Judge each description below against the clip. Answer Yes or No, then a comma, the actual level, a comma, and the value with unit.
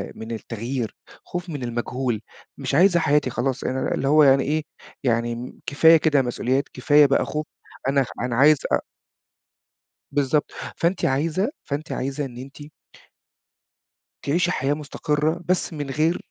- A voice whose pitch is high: No, medium, 140 Hz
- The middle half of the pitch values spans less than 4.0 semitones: Yes, average, 3.2 semitones